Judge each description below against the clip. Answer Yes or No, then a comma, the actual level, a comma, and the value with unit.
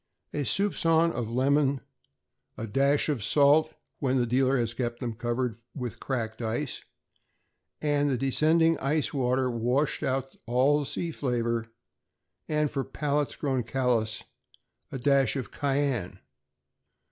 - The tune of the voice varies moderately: Yes, average, 3.2 semitones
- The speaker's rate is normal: No, slow, 130 wpm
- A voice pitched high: No, low, 135 Hz